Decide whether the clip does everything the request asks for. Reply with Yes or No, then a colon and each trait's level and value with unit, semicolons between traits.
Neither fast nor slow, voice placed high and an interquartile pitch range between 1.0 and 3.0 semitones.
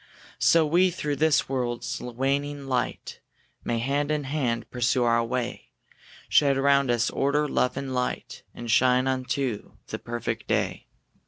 No: average, 145 wpm; low, 130 Hz; average, 2.7 semitones